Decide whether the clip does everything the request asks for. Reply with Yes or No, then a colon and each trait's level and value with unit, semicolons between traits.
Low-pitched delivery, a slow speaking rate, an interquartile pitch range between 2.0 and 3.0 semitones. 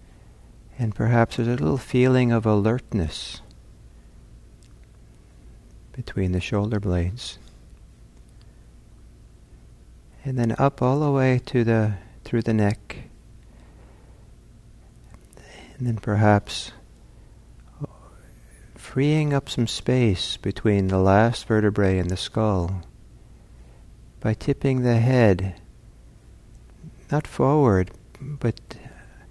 No: low, 110 Hz; slow, 90 wpm; average, 4.4 semitones